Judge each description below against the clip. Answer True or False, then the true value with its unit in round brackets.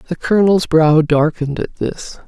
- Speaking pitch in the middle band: True (160 Hz)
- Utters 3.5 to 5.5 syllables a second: True (5.0 syllables/s)